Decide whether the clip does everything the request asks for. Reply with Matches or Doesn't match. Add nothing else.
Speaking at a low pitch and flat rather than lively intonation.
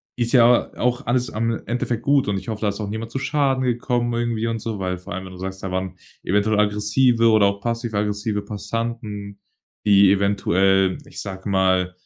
Doesn't match